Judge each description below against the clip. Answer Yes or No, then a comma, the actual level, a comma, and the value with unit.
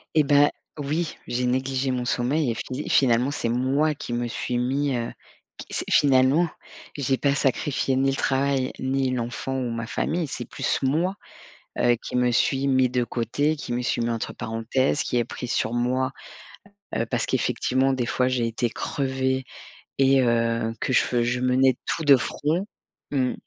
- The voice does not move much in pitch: Yes, narrow, 2.2 semitones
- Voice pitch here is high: No, low, 130 Hz